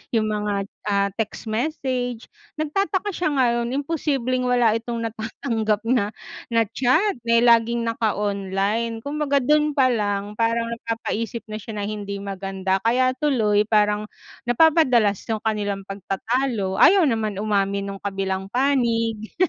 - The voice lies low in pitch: No, high, 225 Hz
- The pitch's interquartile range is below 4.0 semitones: Yes, average, 3.6 semitones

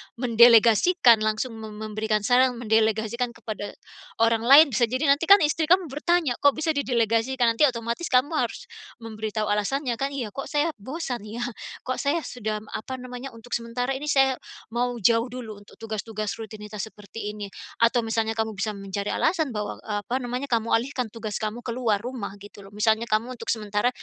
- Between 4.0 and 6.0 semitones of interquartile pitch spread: No, average, 3.2 semitones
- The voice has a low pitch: No, high, 230 Hz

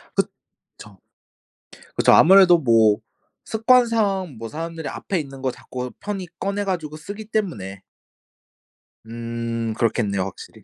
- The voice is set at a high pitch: No, medium, 150 Hz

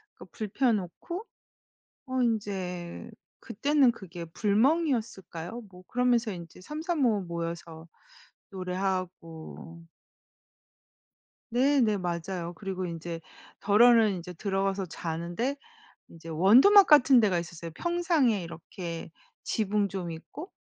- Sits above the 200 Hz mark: No, high, 195 Hz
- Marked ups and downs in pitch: Yes, wide, 6.0 semitones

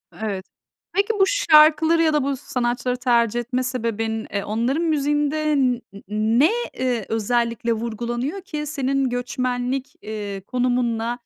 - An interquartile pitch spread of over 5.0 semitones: No, average, 4.0 semitones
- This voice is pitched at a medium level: No, very high, 250 Hz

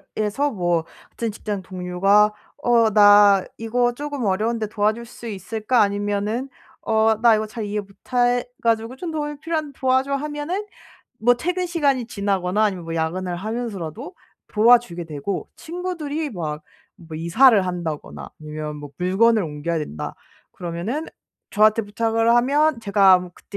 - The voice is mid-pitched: No, high, 215 Hz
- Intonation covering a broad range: No, average, 4.9 semitones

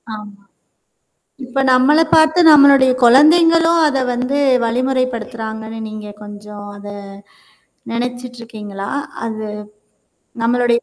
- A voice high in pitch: Yes, high, 245 Hz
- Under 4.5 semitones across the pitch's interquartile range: Yes, average, 3.8 semitones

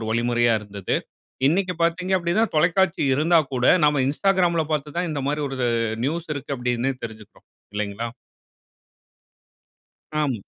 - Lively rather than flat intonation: Yes, wide, 6.2 semitones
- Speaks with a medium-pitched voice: Yes, medium, 145 Hz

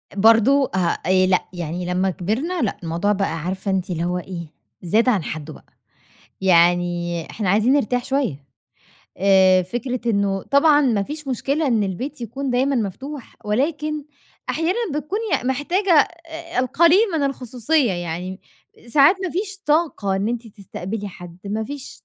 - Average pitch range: No, wide, 7.1 semitones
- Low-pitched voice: No, high, 220 Hz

